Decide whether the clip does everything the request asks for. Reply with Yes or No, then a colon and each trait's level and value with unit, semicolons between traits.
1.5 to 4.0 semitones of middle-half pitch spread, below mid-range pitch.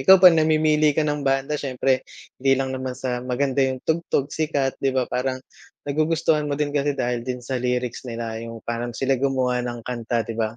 Yes: average, 3.0 semitones; low, 130 Hz